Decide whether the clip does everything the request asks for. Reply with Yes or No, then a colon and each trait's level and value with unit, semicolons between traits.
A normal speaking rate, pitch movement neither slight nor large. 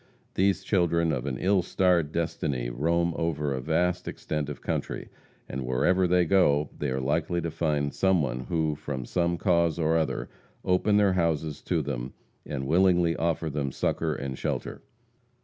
Yes: average, 165 wpm; average, 3.5 semitones